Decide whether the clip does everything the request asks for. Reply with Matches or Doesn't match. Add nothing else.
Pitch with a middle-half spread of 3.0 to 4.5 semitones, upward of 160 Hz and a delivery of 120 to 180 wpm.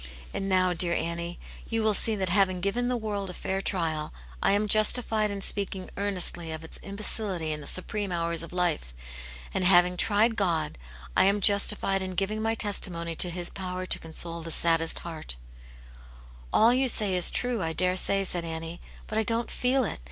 Doesn't match